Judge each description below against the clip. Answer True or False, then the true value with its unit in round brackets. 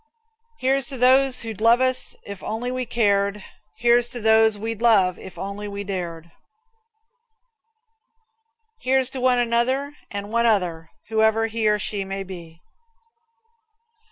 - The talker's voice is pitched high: True (220 Hz)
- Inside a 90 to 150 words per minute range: True (135 wpm)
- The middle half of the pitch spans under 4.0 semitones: True (3.5 semitones)